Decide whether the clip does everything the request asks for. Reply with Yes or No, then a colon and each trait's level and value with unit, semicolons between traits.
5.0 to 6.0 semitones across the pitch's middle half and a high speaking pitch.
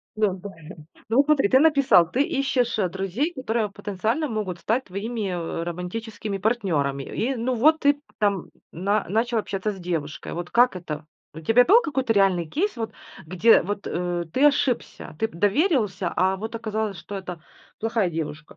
Yes: average, 5.3 semitones; high, 210 Hz